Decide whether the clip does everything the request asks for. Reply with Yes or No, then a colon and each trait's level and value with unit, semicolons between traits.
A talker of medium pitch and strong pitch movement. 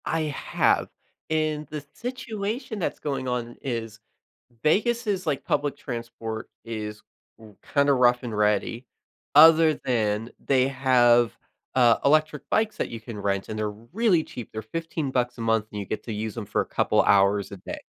No: low, 125 Hz; wide, 5.9 semitones